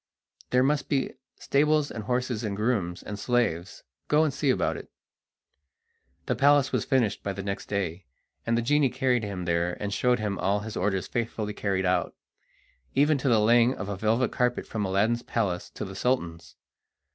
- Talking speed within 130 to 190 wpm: Yes, average, 180 wpm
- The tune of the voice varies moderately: Yes, average, 4.4 semitones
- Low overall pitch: Yes, low, 110 Hz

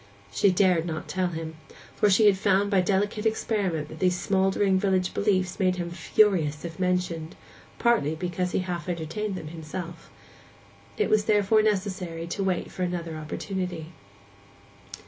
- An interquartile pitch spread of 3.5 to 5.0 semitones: No, average, 2.9 semitones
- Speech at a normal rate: Yes, average, 150 wpm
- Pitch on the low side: No, medium, 185 Hz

